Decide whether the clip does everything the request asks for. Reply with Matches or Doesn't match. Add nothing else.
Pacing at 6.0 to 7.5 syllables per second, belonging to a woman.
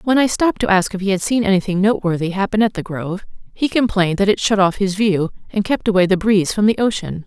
Matches